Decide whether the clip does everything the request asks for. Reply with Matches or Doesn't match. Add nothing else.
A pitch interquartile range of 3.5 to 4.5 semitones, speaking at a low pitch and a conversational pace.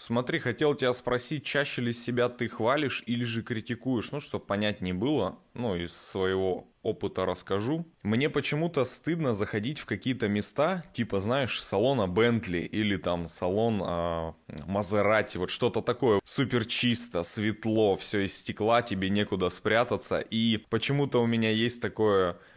Matches